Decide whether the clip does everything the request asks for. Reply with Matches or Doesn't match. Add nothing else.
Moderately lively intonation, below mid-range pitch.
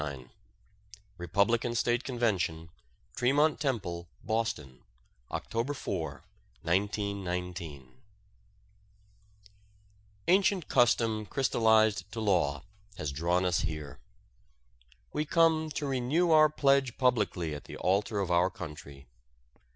Doesn't match